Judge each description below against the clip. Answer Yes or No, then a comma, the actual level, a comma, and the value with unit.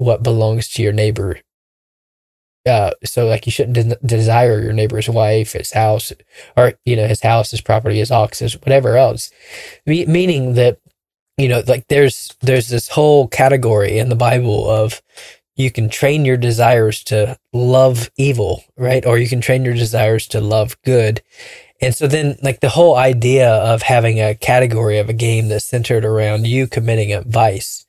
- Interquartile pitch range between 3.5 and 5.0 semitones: No, average, 2.9 semitones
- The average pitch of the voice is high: No, low, 120 Hz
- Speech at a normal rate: Yes, average, 180 wpm